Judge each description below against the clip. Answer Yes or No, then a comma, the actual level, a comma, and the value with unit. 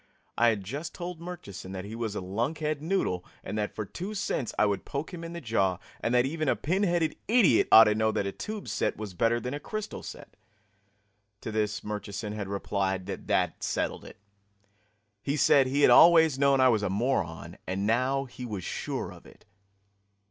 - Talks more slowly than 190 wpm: No, fast, 205 wpm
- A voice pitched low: Yes, low, 120 Hz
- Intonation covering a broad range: Yes, wide, 7.1 semitones